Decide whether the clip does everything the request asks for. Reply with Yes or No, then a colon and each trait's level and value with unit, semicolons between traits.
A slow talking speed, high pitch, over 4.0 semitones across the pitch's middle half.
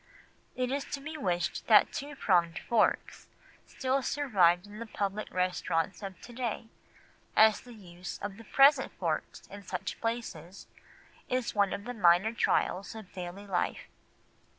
No: average, 150 wpm; high, 205 Hz; average, 5.1 semitones